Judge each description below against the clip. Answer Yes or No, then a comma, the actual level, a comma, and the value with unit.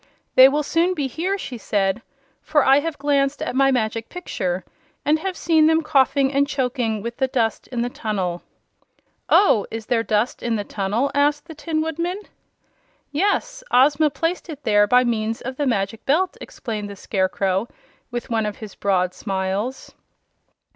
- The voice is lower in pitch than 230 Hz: No, very high, 255 Hz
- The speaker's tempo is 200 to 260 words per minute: No, average, 175 wpm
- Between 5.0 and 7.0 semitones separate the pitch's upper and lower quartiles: Yes, wide, 5.6 semitones